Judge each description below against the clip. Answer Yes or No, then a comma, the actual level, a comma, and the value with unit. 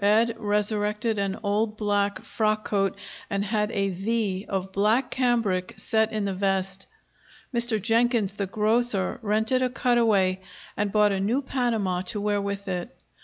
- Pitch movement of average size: No, narrow, 2.3 semitones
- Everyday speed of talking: Yes, average, 155 wpm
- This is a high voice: Yes, high, 210 Hz